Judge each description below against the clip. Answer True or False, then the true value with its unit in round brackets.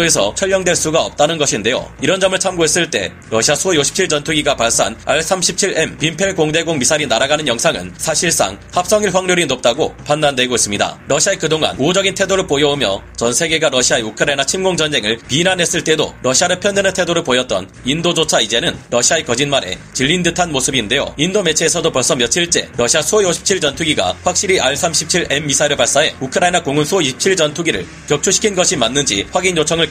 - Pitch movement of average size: True (4.5 semitones)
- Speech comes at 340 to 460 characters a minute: True (415 characters per minute)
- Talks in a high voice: False (160 Hz)